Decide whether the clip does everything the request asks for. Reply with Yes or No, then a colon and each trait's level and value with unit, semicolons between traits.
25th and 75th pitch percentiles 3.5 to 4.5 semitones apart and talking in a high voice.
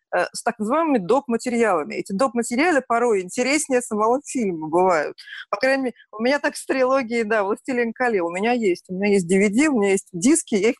Yes: average, 4.1 semitones; high, 235 Hz